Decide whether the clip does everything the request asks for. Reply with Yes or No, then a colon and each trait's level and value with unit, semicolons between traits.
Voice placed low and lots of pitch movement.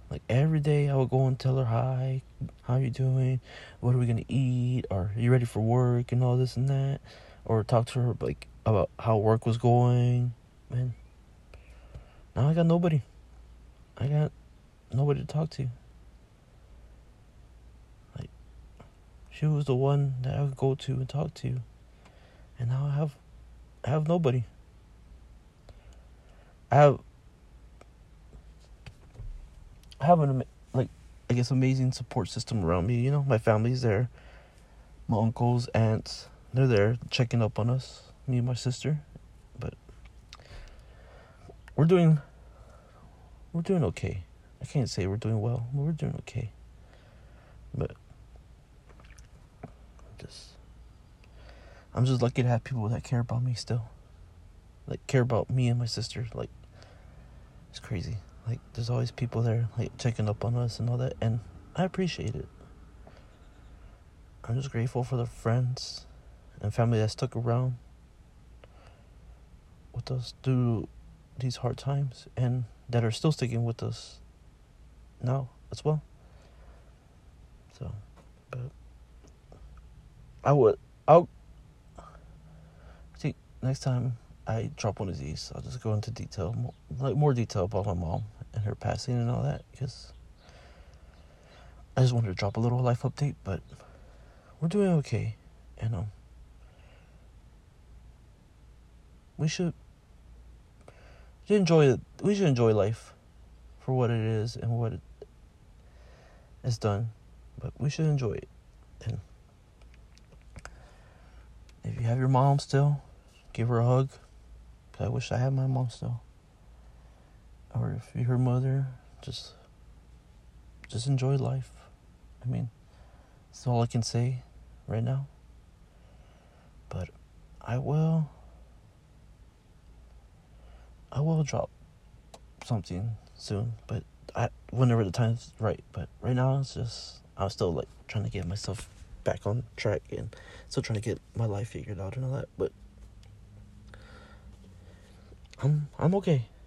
Yes: low, 115 Hz; wide, 7.2 semitones